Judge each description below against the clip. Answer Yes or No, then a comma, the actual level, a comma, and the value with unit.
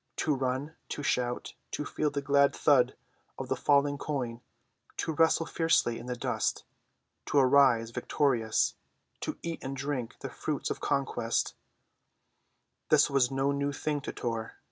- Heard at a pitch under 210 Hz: Yes, medium, 140 Hz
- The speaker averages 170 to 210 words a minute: No, average, 145 wpm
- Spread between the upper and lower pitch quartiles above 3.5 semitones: No, average, 2.8 semitones